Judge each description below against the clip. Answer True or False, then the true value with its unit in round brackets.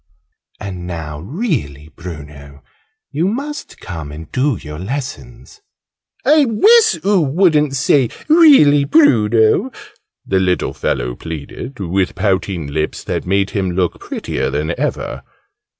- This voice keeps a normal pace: False (120 wpm)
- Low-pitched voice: True (100 Hz)